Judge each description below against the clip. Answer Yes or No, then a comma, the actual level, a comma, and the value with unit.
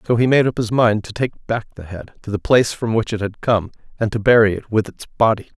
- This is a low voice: Yes, low, 110 Hz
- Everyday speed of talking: No, fast, 280 wpm